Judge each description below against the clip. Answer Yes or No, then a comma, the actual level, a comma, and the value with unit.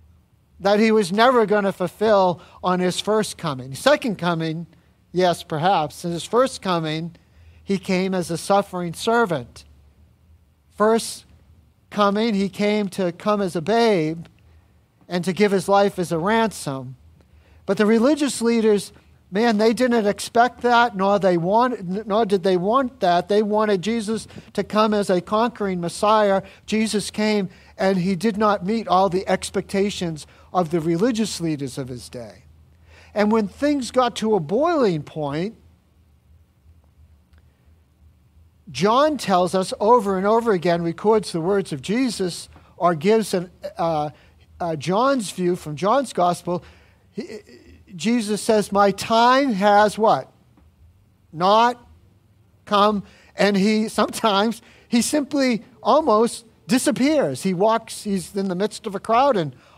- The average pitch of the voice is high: Yes, high, 195 Hz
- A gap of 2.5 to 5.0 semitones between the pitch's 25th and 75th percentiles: No, wide, 5.4 semitones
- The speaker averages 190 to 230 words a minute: No, average, 140 wpm